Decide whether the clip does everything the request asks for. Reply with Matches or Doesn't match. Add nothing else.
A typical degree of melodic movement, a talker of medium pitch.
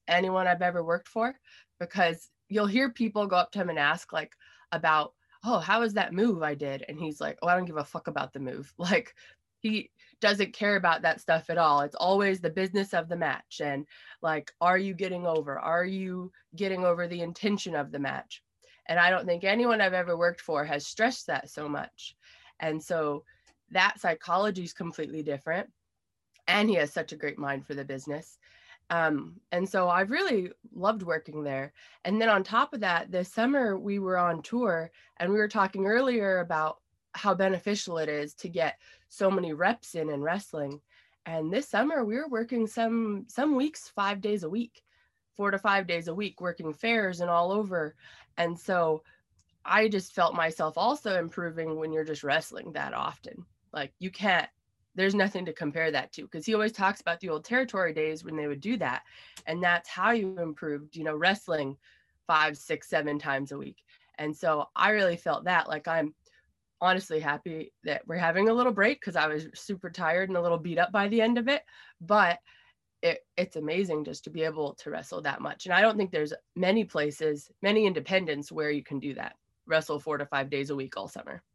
Matches